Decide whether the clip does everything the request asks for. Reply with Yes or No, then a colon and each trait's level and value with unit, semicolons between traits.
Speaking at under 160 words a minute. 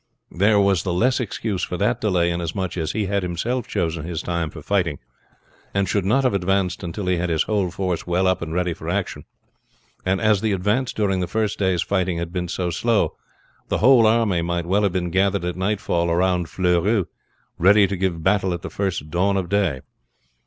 No: fast, 205 wpm